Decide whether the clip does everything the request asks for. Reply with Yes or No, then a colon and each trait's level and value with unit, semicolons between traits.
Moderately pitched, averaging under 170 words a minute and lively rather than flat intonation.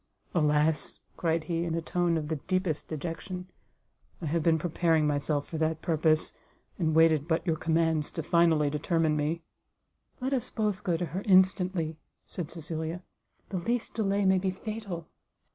No: medium, 165 Hz; average, 160 wpm; narrow, 2.5 semitones